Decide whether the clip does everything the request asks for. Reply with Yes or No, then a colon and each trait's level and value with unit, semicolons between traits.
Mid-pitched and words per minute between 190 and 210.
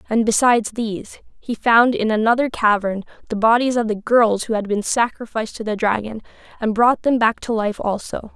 No: high, 225 Hz; average, 195 wpm